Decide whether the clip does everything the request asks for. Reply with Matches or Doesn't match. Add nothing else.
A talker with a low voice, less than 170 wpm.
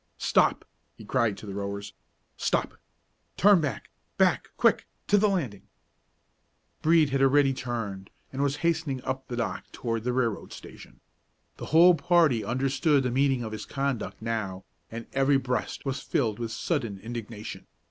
Matches